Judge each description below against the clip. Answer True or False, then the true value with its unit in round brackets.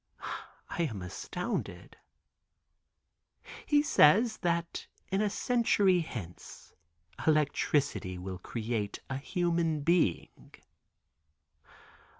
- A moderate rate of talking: False (80 wpm)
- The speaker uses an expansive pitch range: True (8.7 semitones)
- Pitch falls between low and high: True (160 Hz)